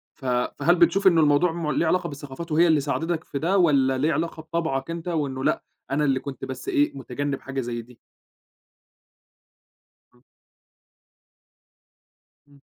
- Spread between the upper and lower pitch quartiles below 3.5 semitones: No, average, 3.8 semitones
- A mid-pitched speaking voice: Yes, medium, 145 Hz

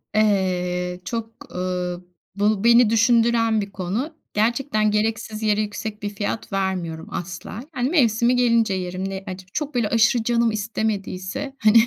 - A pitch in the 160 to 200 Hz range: No, high, 215 Hz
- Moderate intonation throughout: Yes, average, 3.5 semitones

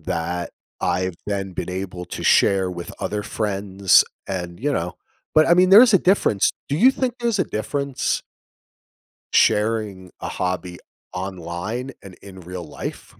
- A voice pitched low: Yes, low, 100 Hz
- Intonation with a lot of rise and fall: Yes, wide, 6.5 semitones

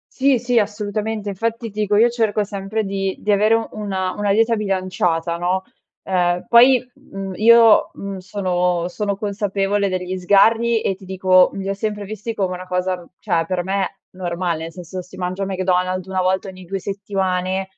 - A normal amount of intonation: No, narrow, 2.3 semitones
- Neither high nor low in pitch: No, high, 195 Hz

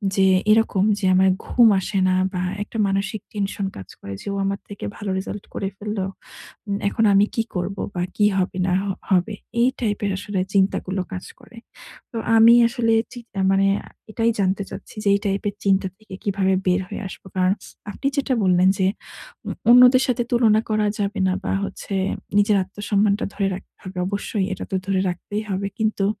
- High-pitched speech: Yes, high, 200 Hz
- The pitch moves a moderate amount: No, narrow, 2.1 semitones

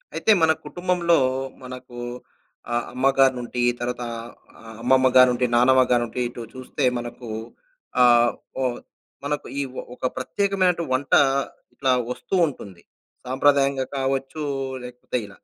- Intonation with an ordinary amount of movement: No, narrow, 2.3 semitones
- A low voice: Yes, low, 130 Hz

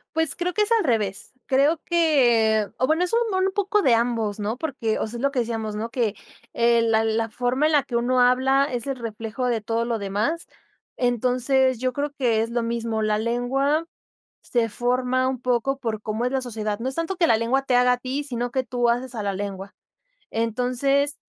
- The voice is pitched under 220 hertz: No, high, 245 Hz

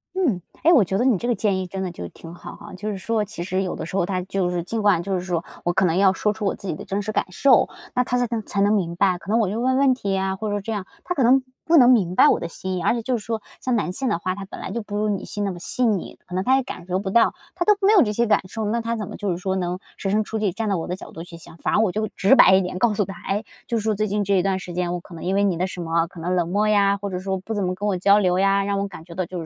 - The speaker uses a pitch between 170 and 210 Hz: Yes, high, 195 Hz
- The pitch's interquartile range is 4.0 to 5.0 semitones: No, average, 2.9 semitones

